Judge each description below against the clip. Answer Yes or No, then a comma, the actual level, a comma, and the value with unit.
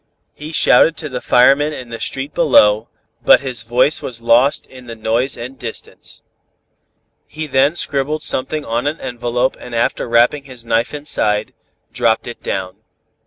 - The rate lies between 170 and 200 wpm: No, average, 160 wpm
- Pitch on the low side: Yes, low, 125 Hz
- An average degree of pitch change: Yes, average, 3.3 semitones